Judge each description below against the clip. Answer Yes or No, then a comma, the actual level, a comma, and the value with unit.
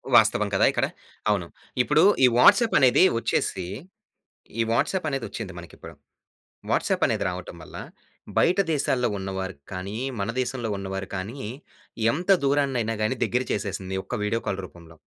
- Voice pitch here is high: No, low, 115 Hz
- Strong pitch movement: Yes, wide, 5.7 semitones